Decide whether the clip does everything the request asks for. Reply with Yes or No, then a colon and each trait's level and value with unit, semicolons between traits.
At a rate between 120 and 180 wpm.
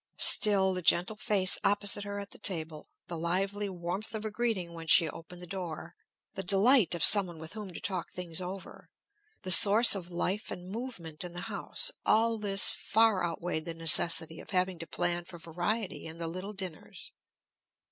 No: average, 190 wpm